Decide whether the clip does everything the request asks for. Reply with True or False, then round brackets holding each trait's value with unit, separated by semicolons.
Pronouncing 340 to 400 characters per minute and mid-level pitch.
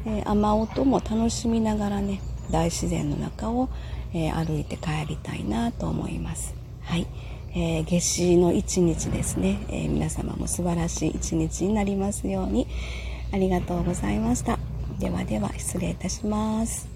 False (295 characters per minute; 170 Hz)